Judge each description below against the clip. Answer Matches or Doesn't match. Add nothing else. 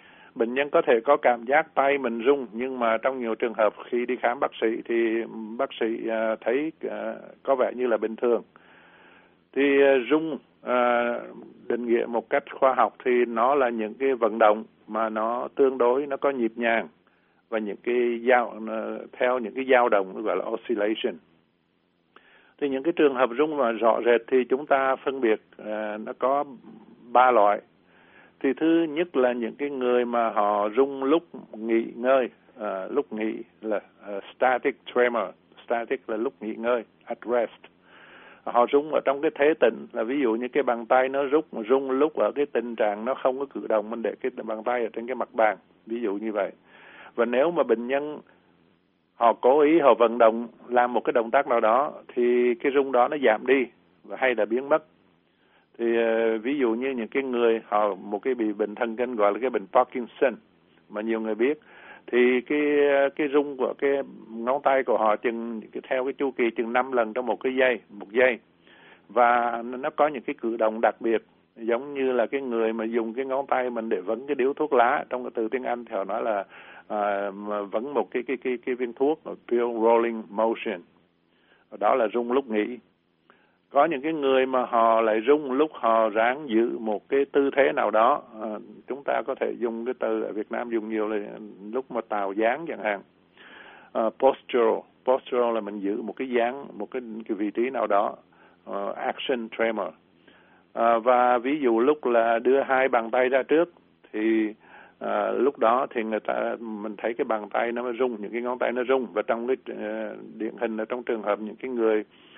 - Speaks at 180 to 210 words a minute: Matches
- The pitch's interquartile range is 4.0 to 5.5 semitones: Doesn't match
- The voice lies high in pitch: Doesn't match